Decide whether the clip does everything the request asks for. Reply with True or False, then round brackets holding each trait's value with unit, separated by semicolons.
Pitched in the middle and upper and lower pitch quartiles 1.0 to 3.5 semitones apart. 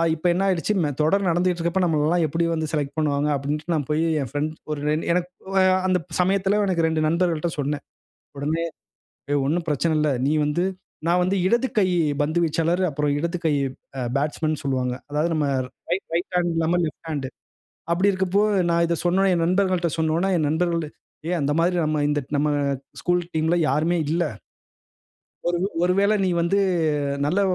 True (165 Hz; 2.8 semitones)